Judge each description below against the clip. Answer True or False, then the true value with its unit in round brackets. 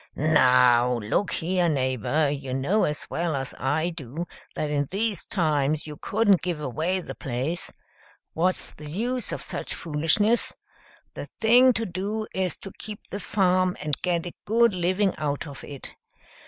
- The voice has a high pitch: False (165 Hz)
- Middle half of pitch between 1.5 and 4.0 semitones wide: False (5.0 semitones)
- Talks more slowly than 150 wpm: False (160 wpm)